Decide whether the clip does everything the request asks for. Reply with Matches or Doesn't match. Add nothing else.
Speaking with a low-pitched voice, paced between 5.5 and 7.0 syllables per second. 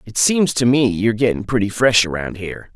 Matches